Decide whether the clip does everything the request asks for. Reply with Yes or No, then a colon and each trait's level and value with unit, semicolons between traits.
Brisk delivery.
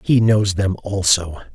No: average, 155 wpm